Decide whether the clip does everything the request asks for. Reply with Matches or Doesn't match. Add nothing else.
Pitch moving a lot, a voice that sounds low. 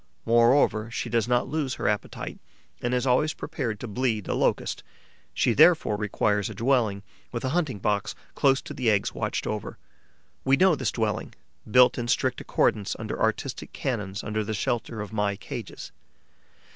Doesn't match